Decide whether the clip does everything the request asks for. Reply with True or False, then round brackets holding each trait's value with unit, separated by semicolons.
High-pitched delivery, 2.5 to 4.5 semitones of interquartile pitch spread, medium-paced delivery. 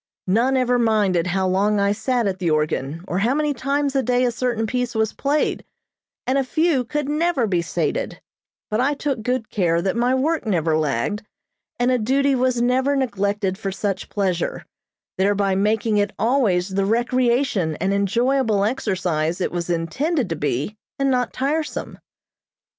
False (220 Hz; 5.3 semitones; 170 wpm)